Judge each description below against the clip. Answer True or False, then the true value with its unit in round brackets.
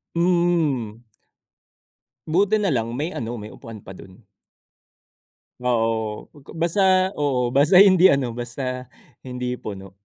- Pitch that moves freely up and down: True (7.0 semitones)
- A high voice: False (125 Hz)